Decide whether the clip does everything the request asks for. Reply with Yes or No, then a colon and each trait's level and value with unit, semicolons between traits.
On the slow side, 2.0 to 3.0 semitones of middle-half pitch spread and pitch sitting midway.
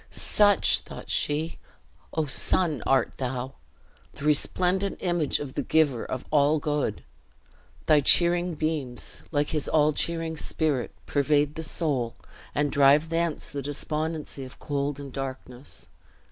Yes: slow, 130 wpm; narrow, 2.6 semitones; medium, 150 Hz